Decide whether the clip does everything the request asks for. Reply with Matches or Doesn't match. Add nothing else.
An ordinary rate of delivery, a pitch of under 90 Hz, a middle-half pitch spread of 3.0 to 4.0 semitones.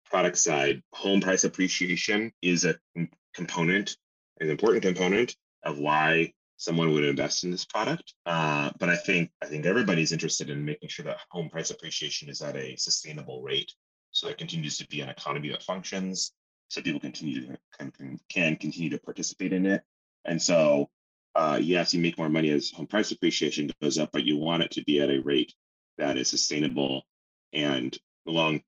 Matches